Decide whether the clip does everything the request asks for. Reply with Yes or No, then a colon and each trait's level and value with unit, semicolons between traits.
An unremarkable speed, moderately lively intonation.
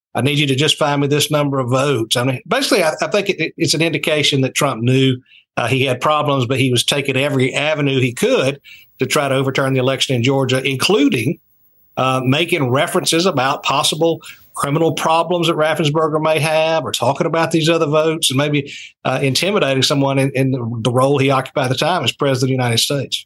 No: fast, 215 wpm; average, 3.1 semitones